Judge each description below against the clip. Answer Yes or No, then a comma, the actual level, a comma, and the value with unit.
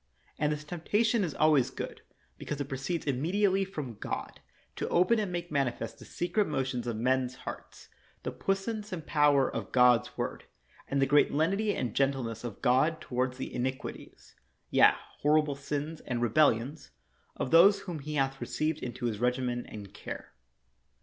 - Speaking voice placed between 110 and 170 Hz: Yes, medium, 140 Hz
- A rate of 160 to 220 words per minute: Yes, average, 170 wpm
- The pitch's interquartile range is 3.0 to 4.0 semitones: No, average, 4.7 semitones